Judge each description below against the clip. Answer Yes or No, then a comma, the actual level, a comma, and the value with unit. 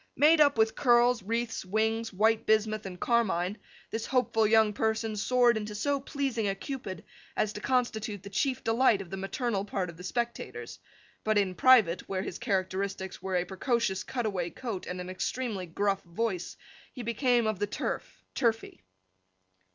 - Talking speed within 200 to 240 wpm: No, average, 165 wpm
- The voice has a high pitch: Yes, high, 215 Hz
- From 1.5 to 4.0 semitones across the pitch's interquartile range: Yes, average, 3.7 semitones